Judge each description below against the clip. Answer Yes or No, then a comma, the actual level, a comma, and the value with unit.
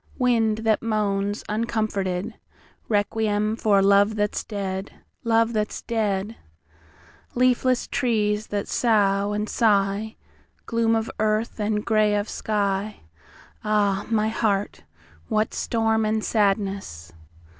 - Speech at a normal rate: No, slow, 90 wpm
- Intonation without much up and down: Yes, narrow, 1.9 semitones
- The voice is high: Yes, high, 210 Hz